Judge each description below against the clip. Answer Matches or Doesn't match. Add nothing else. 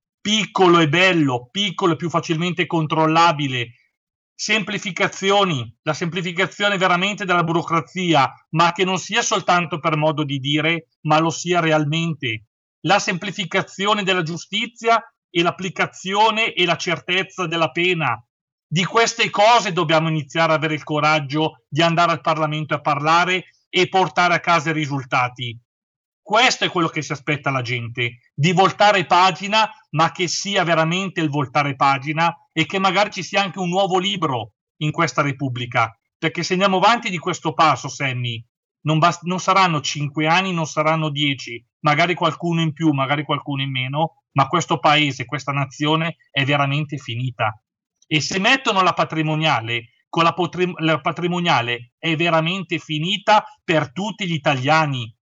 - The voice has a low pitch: Doesn't match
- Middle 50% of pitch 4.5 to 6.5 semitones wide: Doesn't match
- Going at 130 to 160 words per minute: Matches